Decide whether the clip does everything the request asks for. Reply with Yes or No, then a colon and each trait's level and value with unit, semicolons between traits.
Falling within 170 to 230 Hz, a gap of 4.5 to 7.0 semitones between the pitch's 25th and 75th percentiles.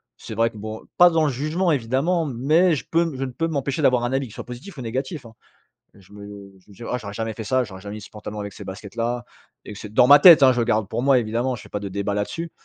No: low, 120 Hz; average, 4.8 semitones